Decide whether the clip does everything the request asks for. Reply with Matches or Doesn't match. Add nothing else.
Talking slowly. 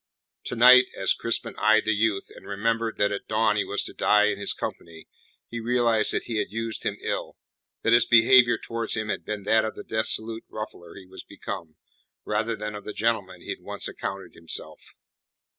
Doesn't match